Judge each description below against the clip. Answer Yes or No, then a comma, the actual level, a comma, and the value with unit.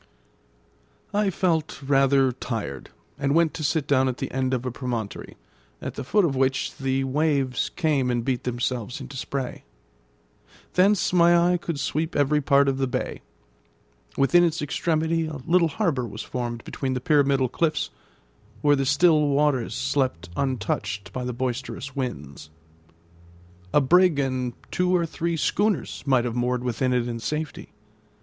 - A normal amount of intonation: Yes, average, 3.9 semitones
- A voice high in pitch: No, low, 135 Hz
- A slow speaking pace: No, average, 155 wpm